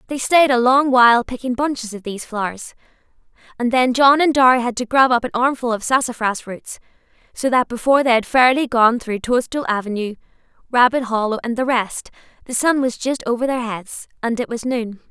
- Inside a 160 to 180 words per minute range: No, average, 200 wpm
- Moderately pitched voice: No, high, 245 Hz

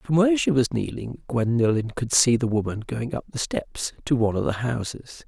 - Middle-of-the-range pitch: No, low, 115 Hz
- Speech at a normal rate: No, fast, 215 wpm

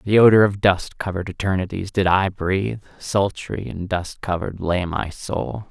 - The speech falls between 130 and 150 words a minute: No, average, 170 wpm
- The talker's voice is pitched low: Yes, very low, 95 Hz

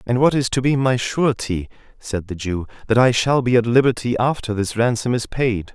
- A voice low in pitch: Yes, low, 120 Hz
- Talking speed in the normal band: No, fast, 220 wpm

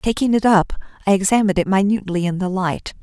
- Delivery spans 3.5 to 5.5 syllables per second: No, 6.5 syllables/s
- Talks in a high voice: Yes, high, 195 Hz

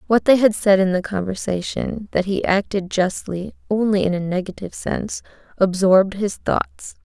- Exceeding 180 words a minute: No, average, 160 wpm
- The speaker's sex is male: No, female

